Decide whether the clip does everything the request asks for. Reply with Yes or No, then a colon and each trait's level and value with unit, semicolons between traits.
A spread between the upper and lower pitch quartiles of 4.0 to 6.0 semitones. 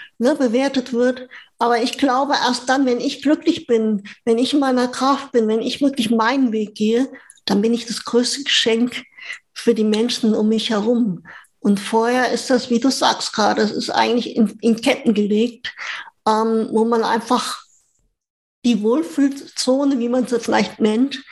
No: average, 2.7 semitones